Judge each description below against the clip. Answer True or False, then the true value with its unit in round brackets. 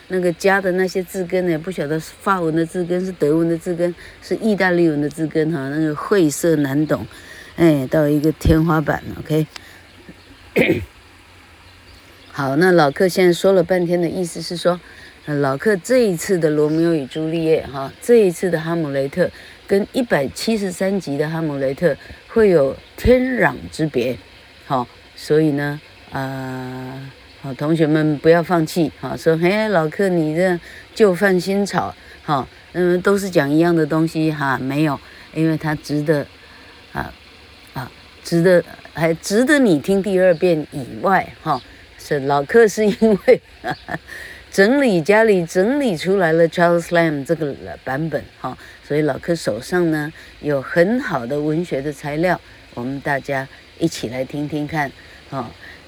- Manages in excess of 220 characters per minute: True (240 characters per minute)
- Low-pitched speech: False (160 Hz)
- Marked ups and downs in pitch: False (4.2 semitones)